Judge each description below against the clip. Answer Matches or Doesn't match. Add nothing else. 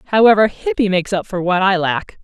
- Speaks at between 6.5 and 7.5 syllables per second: Doesn't match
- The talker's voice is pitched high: Matches